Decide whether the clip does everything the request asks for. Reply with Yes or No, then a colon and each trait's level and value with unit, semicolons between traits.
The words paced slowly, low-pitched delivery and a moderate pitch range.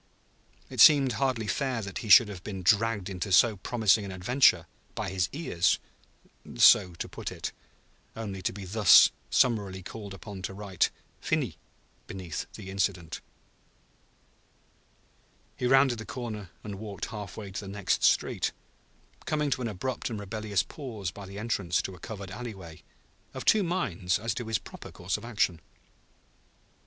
No: average, 160 wpm; low, 105 Hz; average, 3.4 semitones